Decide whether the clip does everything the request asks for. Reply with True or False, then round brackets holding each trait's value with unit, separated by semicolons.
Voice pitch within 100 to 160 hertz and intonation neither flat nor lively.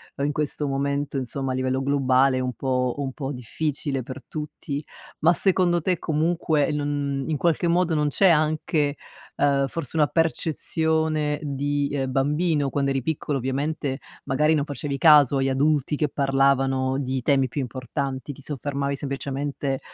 False (140 Hz; 2.1 semitones)